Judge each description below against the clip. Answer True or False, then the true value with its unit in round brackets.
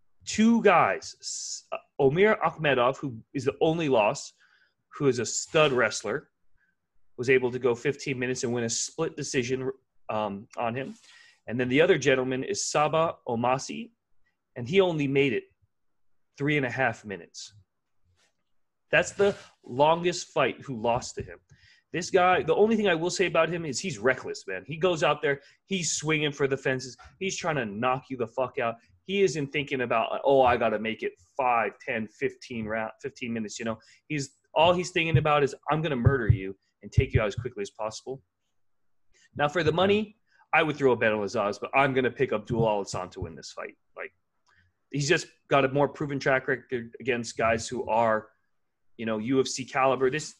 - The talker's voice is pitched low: True (130 Hz)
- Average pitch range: False (5.7 semitones)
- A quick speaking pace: False (190 wpm)